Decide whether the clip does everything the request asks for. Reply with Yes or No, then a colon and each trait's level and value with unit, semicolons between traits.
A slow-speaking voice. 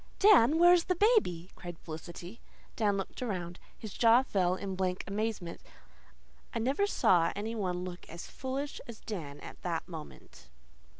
No: average, 155 wpm